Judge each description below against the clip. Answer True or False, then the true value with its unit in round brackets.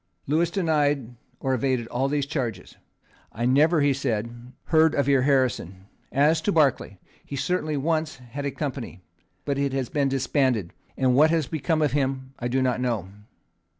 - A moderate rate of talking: True (170 wpm)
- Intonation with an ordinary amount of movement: True (3.1 semitones)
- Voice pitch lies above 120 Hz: True (135 Hz)